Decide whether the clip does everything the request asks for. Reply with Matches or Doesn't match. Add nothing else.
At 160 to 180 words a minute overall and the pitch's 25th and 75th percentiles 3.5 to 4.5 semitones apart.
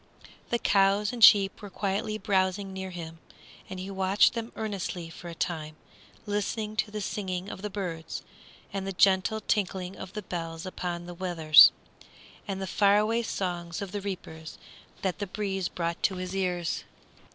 Doesn't match